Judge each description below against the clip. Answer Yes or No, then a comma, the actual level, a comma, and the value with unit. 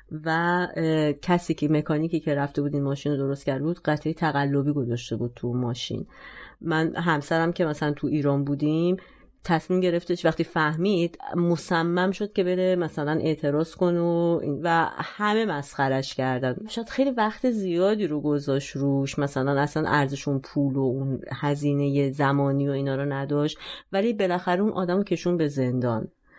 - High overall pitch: No, medium, 155 Hz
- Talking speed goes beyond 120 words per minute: Yes, fast, 155 wpm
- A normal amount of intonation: Yes, average, 3.8 semitones